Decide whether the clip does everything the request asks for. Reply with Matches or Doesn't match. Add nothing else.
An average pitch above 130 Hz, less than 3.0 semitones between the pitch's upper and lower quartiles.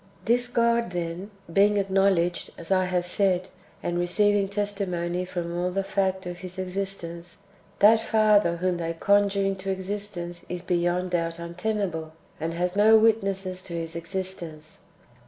Matches